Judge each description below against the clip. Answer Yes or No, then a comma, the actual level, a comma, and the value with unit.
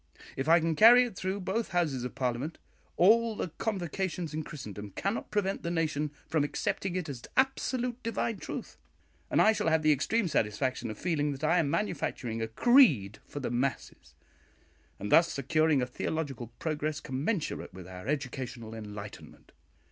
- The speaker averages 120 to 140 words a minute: No, average, 165 wpm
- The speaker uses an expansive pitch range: Yes, wide, 6.7 semitones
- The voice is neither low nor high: Yes, medium, 155 Hz